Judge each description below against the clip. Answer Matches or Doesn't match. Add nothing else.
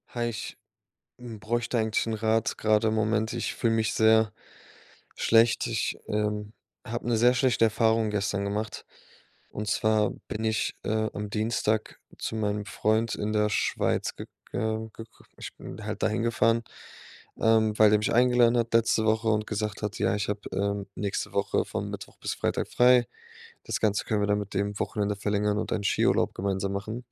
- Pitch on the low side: Matches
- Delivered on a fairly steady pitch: Matches